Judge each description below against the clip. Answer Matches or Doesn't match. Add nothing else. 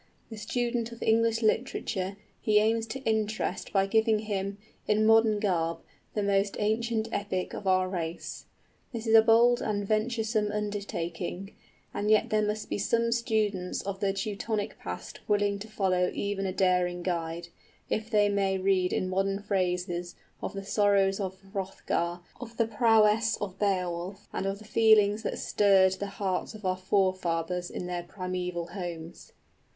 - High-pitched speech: Matches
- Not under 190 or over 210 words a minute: Doesn't match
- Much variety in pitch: Doesn't match